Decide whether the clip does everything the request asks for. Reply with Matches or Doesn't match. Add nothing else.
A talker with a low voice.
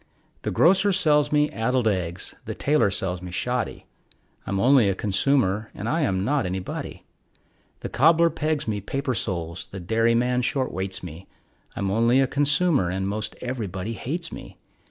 Matches